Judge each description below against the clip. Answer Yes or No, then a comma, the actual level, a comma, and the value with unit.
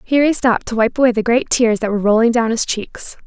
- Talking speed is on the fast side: Yes, fast, 275 wpm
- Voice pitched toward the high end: Yes, high, 235 Hz